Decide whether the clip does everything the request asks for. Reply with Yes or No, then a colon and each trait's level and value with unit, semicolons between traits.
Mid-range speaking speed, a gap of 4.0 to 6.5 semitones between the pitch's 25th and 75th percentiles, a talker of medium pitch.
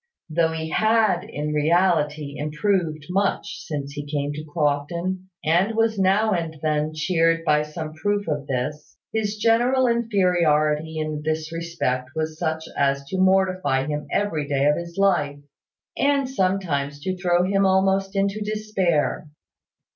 Yes: average, 145 wpm; average, 4.4 semitones; medium, 165 Hz